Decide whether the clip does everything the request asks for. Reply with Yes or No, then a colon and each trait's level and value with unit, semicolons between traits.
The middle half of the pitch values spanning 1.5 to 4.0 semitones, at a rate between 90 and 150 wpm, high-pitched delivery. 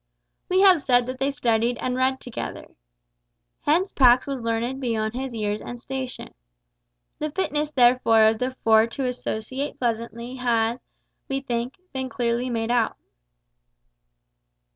Yes: narrow, 2.5 semitones; average, 140 wpm; high, 245 Hz